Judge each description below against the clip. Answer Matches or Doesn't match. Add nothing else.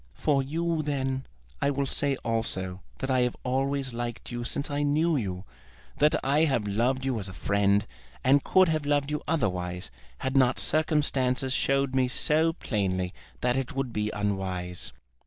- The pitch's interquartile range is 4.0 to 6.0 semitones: Matches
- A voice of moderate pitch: Doesn't match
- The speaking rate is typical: Matches